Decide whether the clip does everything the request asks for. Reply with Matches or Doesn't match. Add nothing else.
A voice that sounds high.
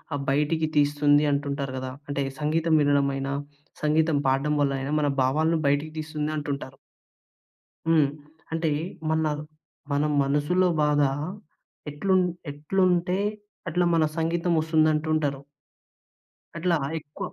Doesn't match